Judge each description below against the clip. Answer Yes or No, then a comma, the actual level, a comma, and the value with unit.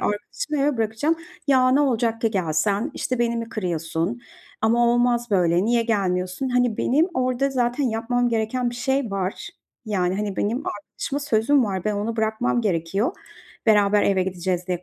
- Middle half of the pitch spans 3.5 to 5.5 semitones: Yes, average, 3.9 semitones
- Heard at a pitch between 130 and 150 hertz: No, high, 225 Hz